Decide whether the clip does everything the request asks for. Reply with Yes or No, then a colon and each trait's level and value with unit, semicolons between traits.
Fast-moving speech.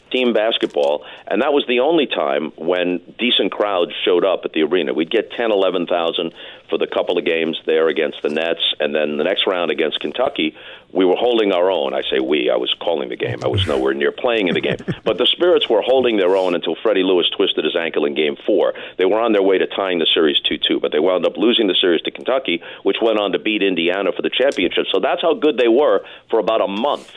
Yes: fast, 245 wpm